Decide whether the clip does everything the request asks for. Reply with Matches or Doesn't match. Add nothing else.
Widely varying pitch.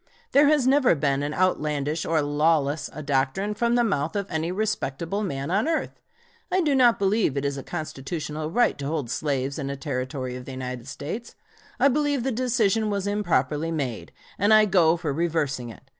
Matches